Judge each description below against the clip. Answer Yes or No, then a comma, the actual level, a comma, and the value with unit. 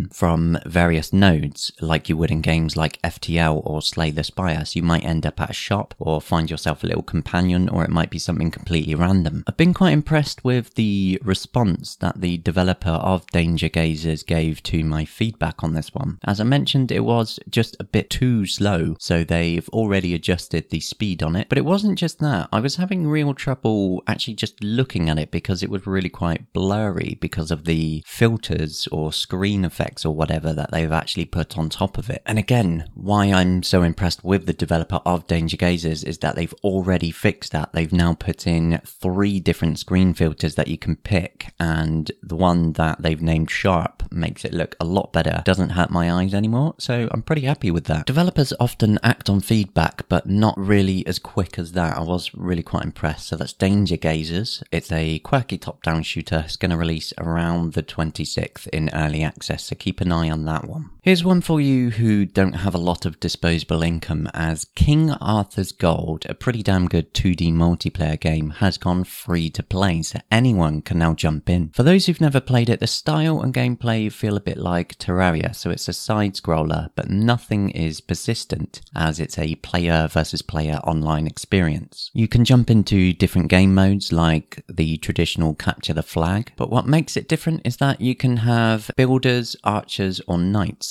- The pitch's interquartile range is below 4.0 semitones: No, average, 4.9 semitones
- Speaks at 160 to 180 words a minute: No, average, 200 wpm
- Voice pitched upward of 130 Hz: No, very low, 90 Hz